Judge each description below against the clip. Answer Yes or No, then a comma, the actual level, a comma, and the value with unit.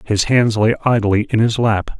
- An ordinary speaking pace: No, fast, 210 wpm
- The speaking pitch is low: Yes, low, 110 Hz